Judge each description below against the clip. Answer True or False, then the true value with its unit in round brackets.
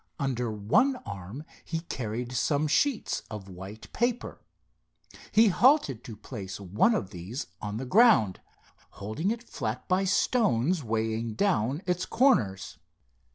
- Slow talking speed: True (130 wpm)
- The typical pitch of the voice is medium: False (125 Hz)